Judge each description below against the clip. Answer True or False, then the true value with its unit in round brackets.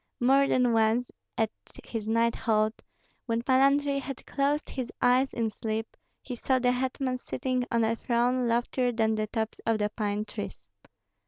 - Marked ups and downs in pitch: False (2.5 semitones)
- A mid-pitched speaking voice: False (240 Hz)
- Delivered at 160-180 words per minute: True (170 wpm)